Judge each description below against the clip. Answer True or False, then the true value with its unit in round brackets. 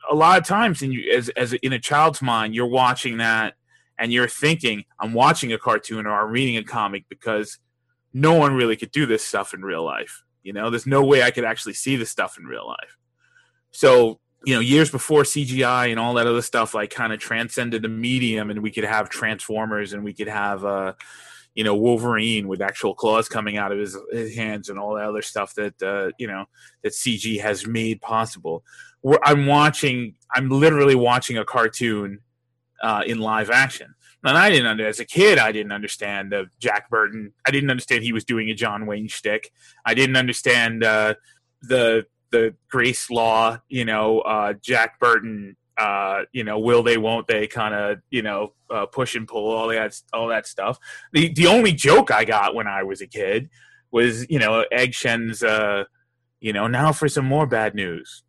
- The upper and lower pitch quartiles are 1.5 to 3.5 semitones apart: True (3.0 semitones)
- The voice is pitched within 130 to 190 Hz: False (115 Hz)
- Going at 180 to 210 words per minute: True (200 wpm)